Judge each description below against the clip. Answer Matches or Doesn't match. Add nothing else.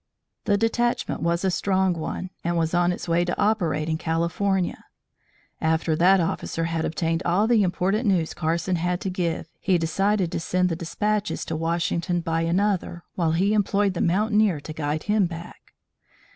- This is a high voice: Doesn't match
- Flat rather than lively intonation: Doesn't match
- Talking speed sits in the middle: Matches